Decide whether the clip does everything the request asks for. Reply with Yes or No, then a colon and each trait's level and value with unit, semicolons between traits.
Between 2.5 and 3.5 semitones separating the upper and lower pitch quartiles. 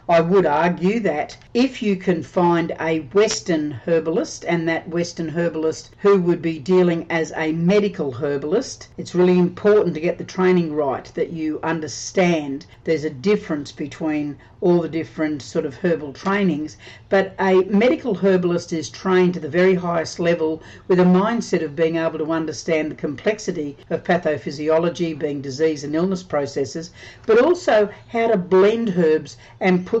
Yes: average, 3.1 semitones